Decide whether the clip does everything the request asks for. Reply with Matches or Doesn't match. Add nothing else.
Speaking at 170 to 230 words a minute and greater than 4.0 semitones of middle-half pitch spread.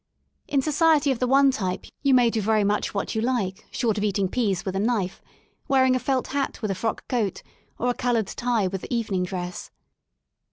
Matches